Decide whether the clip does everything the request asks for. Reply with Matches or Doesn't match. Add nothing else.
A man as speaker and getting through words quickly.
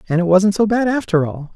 Matches